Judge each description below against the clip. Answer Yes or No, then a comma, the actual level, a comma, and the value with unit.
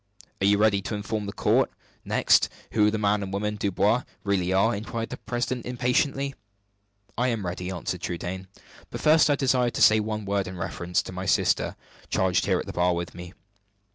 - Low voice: Yes, low, 100 Hz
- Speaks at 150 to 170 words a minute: No, average, 195 wpm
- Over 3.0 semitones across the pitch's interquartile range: Yes, average, 3.6 semitones